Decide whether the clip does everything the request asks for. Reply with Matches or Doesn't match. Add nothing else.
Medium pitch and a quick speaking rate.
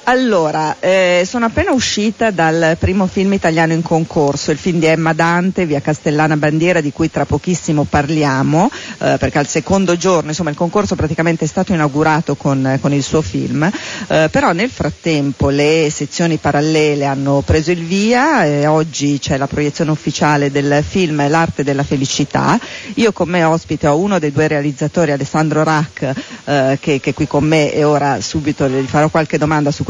Matches